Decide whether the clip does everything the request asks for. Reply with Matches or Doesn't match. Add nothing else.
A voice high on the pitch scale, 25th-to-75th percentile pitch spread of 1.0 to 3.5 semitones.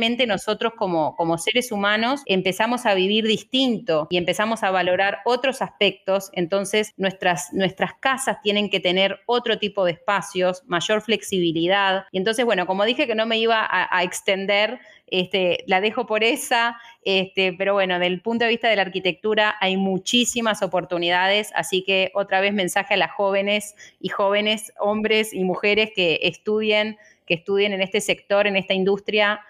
Matches